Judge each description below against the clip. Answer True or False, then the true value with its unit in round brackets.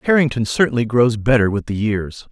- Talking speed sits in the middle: True (180 wpm)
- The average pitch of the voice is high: False (120 Hz)